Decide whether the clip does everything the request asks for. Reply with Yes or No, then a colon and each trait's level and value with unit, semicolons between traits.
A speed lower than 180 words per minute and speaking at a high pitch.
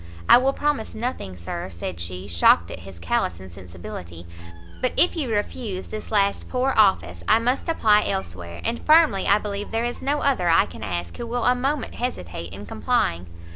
No: average, 185 wpm; high, 200 Hz